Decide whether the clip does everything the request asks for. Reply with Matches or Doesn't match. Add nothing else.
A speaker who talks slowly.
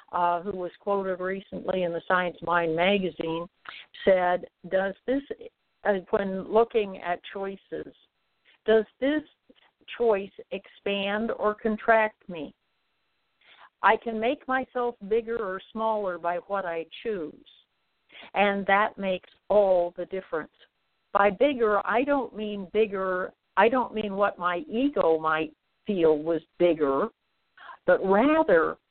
Matches